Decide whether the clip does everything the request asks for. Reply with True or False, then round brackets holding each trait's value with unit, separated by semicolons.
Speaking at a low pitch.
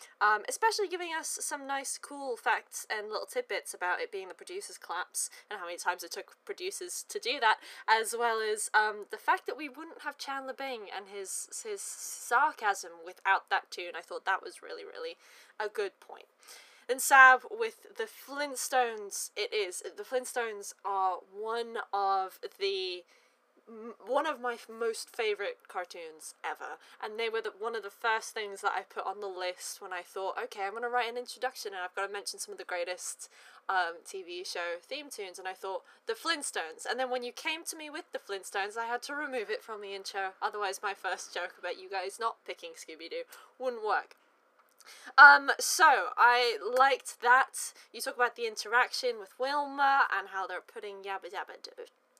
False (260 Hz)